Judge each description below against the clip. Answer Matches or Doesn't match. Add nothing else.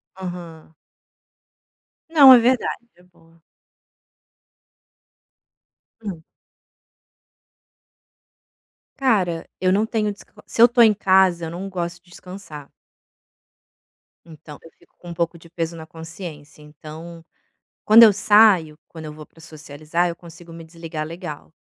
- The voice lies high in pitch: Doesn't match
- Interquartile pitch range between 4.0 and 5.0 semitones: Doesn't match